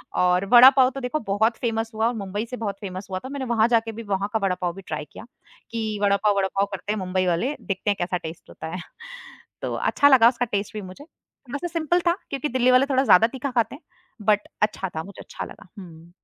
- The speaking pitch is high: Yes, high, 215 Hz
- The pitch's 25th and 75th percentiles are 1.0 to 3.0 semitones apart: No, average, 4.5 semitones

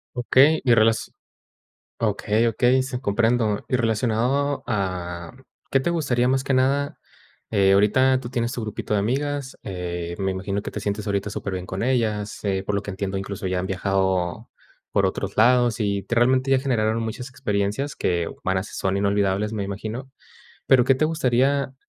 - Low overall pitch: Yes, low, 110 Hz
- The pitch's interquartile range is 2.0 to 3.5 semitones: No, average, 4.6 semitones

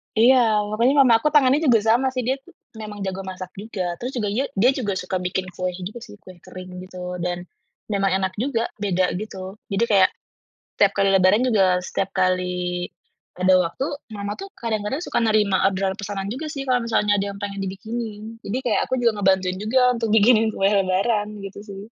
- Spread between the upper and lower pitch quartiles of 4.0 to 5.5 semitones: No, average, 3.6 semitones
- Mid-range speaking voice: No, high, 205 Hz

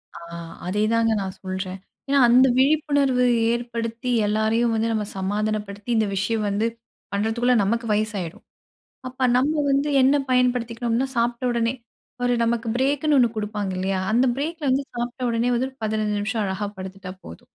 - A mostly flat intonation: No, average, 3.2 semitones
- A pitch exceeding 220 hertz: Yes, high, 230 Hz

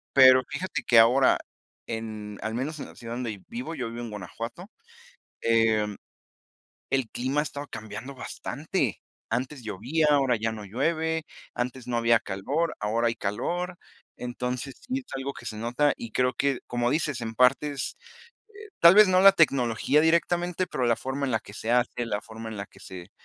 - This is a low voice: Yes, low, 125 Hz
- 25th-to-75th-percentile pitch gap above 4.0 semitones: Yes, average, 4.7 semitones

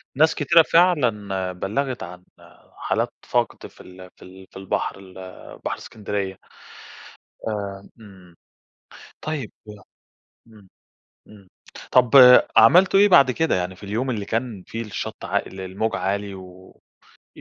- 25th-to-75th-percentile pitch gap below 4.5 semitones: No, average, 5.0 semitones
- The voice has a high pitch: No, low, 105 Hz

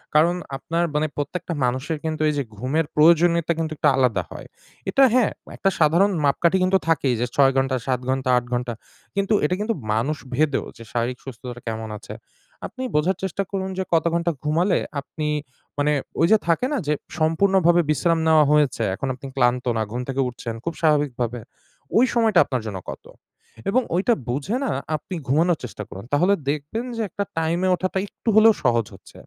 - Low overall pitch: No, medium, 155 Hz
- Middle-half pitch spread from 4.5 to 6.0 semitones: Yes, average, 5.2 semitones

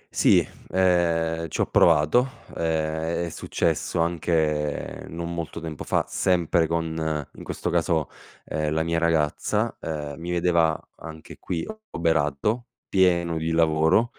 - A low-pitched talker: Yes, very low, 80 Hz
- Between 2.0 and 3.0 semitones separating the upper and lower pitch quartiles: No, narrow, 1.6 semitones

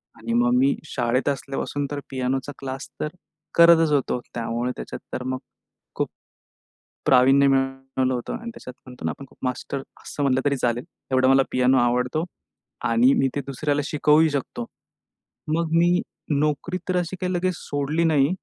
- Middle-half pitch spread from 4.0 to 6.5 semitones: No, average, 3.0 semitones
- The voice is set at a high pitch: No, low, 135 Hz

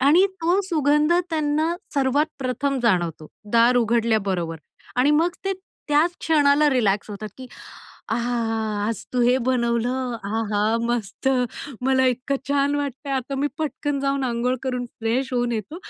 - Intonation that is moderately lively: Yes, average, 3.7 semitones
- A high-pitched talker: Yes, very high, 255 Hz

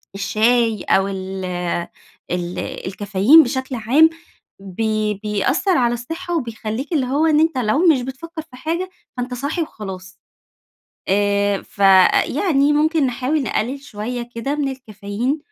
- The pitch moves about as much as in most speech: No, wide, 6.2 semitones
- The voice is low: No, high, 245 Hz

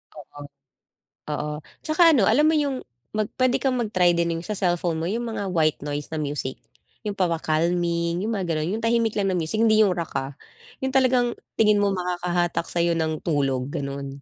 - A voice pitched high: No, medium, 175 Hz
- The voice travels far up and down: Yes, wide, 5.7 semitones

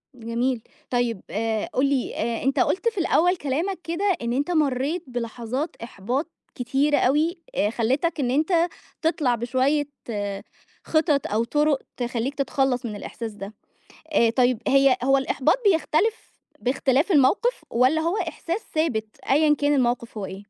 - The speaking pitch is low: No, very high, 270 Hz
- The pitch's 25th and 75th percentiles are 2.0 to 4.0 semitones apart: No, average, 4.6 semitones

